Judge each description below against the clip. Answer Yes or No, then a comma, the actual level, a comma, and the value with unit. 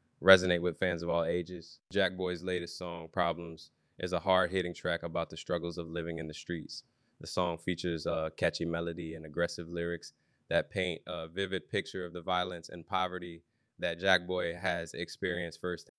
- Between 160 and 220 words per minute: Yes, average, 185 wpm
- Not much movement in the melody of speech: Yes, narrow, 1.3 semitones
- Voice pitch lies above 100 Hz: No, very low, 85 Hz